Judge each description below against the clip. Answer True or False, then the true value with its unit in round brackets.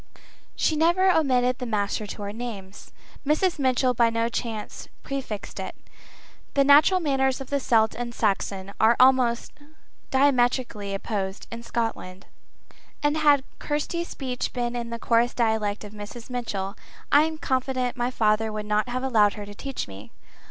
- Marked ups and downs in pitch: False (3.9 semitones)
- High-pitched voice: True (240 Hz)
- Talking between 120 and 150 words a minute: False (160 wpm)